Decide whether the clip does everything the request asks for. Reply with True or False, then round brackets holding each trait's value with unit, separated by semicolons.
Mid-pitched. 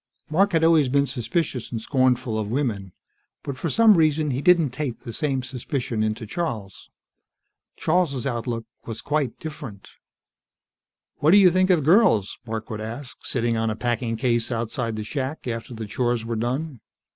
False (125 Hz)